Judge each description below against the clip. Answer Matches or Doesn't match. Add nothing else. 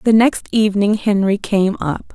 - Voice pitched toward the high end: Matches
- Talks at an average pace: Matches